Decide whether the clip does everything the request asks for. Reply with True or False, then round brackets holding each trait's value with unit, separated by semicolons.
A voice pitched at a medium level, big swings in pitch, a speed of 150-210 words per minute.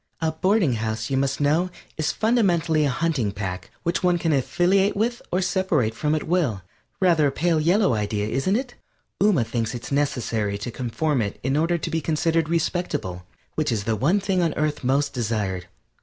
True (150 Hz; 7.0 semitones; 190 wpm)